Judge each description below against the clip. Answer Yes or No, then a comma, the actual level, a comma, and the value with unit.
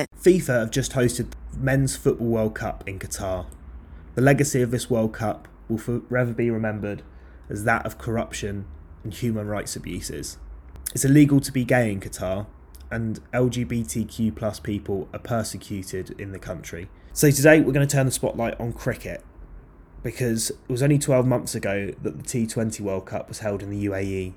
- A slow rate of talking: No, average, 175 wpm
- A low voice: Yes, low, 110 Hz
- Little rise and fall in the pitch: No, average, 4.1 semitones